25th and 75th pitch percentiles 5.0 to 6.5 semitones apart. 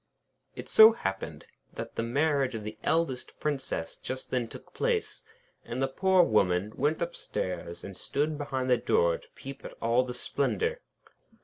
Yes: average, 5.3 semitones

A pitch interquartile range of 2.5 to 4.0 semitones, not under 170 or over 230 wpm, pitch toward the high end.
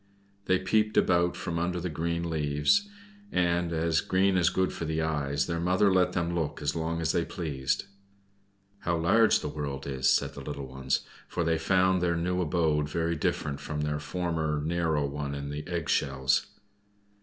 No: average, 3.1 semitones; average, 180 wpm; very low, 80 Hz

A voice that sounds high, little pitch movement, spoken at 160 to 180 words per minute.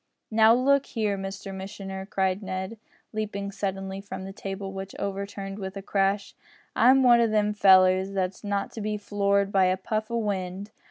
Yes: high, 200 Hz; narrow, 1.5 semitones; average, 175 wpm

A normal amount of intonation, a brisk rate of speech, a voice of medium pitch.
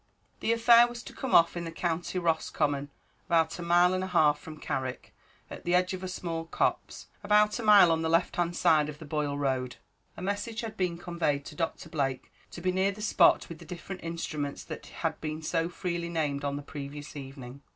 Yes: average, 3.7 semitones; fast, 215 wpm; medium, 165 Hz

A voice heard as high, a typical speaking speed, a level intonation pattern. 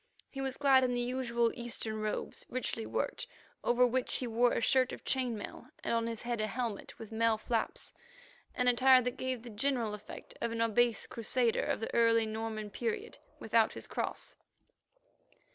Yes: high, 235 Hz; average, 180 wpm; narrow, 2.1 semitones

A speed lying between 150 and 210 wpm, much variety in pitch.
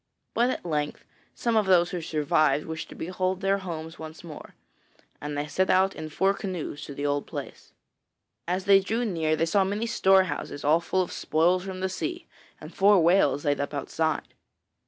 No: average, 190 wpm; average, 3.7 semitones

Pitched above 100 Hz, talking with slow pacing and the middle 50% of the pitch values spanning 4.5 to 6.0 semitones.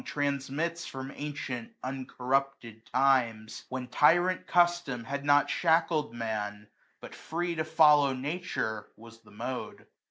Yes: low, 135 Hz; slow, 120 wpm; average, 4.9 semitones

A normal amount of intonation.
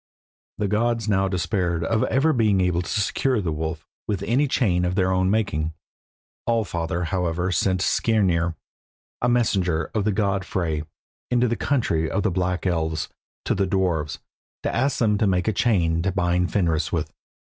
Yes: average, 4.0 semitones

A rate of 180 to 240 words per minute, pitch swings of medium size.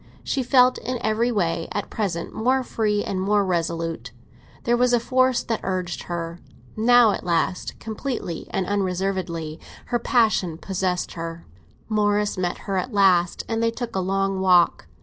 No: average, 160 wpm; average, 4.6 semitones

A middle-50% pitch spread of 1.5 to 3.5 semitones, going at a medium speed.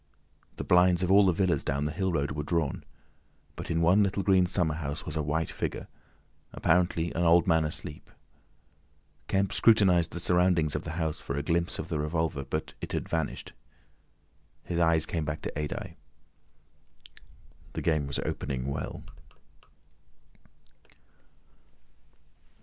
Yes: average, 2.7 semitones; average, 150 wpm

